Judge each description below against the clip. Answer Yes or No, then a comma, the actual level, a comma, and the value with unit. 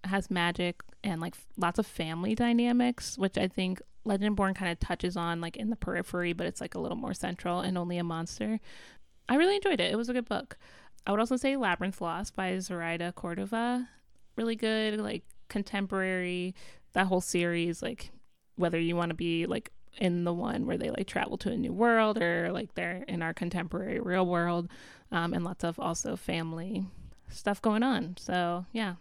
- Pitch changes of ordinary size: Yes, average, 4.2 semitones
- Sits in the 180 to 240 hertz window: Yes, medium, 185 Hz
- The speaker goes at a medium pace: Yes, average, 190 wpm